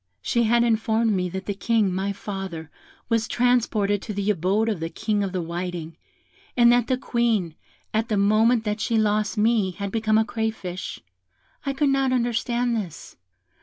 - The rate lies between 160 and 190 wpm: Yes, average, 175 wpm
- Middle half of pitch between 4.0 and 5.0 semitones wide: No, average, 3.3 semitones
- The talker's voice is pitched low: No, high, 215 Hz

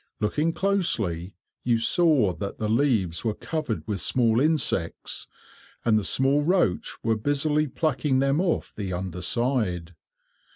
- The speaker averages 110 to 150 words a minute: Yes, slow, 135 wpm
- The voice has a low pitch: Yes, low, 120 Hz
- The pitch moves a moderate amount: No, wide, 6.8 semitones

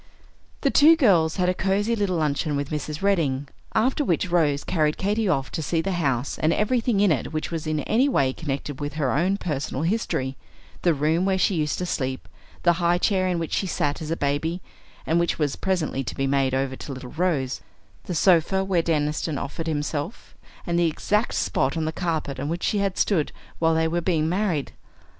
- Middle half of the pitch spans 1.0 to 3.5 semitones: No, average, 4.2 semitones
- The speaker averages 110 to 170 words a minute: No, fast, 205 wpm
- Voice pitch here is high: No, medium, 165 Hz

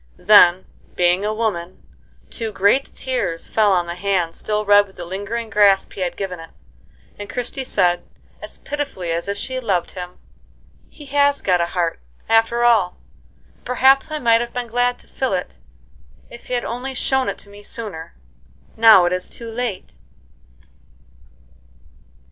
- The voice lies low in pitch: No, high, 210 Hz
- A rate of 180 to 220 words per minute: No, average, 165 wpm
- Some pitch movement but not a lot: Yes, average, 5.0 semitones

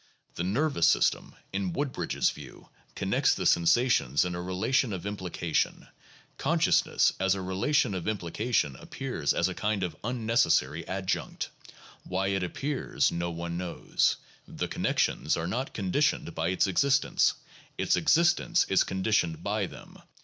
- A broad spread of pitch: Yes, wide, 5.7 semitones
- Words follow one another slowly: No, average, 150 wpm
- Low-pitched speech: Yes, very low, 95 Hz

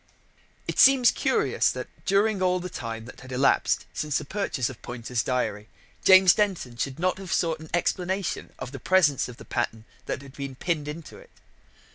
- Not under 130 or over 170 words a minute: No, average, 185 wpm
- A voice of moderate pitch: Yes, medium, 150 Hz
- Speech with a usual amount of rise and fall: No, wide, 6.8 semitones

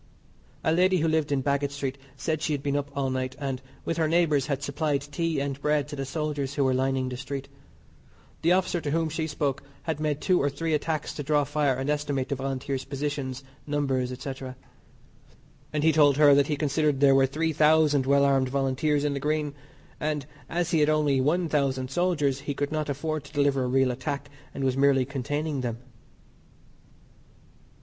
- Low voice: No, medium, 145 Hz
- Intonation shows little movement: Yes, narrow, 2.1 semitones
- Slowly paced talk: No, average, 195 wpm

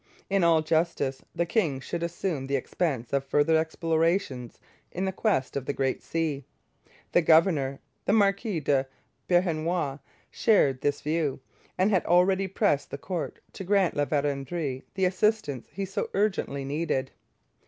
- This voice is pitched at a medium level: Yes, medium, 160 Hz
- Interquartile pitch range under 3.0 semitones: No, average, 4.8 semitones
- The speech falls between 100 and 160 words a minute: Yes, average, 145 wpm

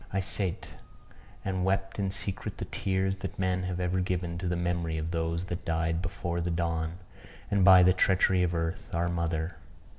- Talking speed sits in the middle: Yes, average, 185 wpm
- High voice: No, very low, 90 Hz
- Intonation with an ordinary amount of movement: No, narrow, 2.0 semitones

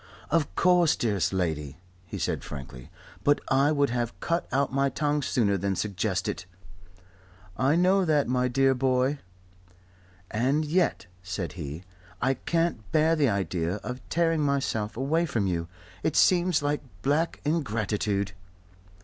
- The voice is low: Yes, low, 130 Hz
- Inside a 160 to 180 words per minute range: No, average, 140 wpm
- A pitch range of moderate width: No, wide, 7.3 semitones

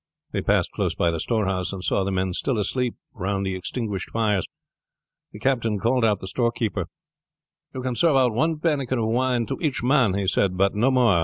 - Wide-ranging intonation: No, average, 4.7 semitones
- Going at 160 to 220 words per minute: Yes, fast, 205 wpm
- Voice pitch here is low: Yes, low, 110 Hz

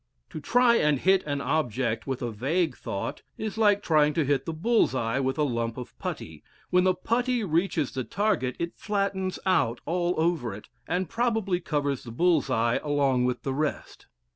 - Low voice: No, medium, 155 Hz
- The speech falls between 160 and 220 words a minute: Yes, average, 190 wpm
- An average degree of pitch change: No, wide, 6.4 semitones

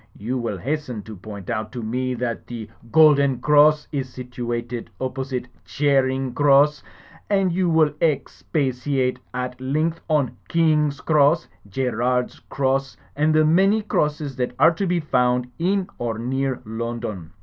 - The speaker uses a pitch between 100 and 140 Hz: Yes, low, 135 Hz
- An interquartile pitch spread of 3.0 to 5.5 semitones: Yes, average, 3.7 semitones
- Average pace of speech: Yes, average, 150 wpm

